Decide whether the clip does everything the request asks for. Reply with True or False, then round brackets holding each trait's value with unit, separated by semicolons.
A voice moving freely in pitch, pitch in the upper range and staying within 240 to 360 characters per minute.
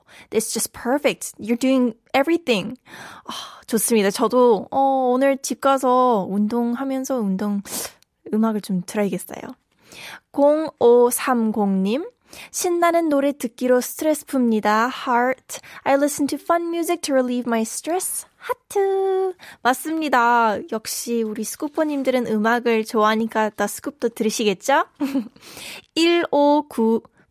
False (4.2 semitones; 250 Hz; 335 characters per minute)